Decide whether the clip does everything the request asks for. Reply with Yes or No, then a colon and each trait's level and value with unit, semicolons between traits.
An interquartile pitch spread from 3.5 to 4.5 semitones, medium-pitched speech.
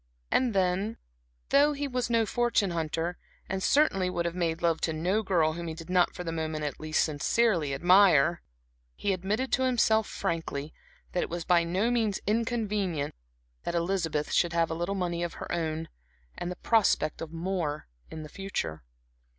Yes: average, 3.9 semitones; medium, 175 Hz